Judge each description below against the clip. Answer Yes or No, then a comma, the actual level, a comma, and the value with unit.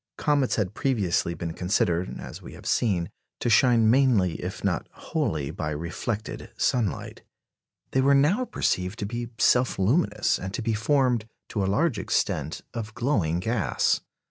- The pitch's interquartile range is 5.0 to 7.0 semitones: Yes, wide, 5.5 semitones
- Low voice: Yes, low, 110 Hz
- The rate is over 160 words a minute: No, average, 155 wpm